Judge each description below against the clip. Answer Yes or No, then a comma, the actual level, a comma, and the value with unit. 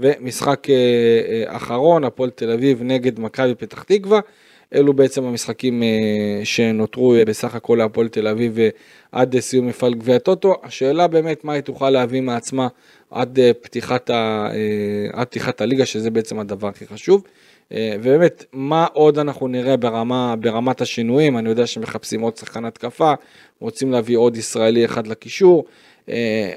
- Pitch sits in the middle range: No, low, 120 Hz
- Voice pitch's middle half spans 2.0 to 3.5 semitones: Yes, average, 2.8 semitones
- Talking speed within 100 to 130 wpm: No, average, 140 wpm